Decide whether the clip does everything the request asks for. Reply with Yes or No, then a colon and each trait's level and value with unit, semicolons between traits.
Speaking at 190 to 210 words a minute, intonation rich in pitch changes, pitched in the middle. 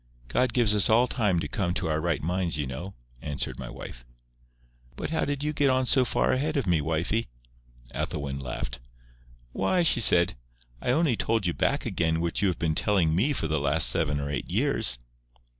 No: fast, 205 wpm; wide, 8.0 semitones; very low, 85 Hz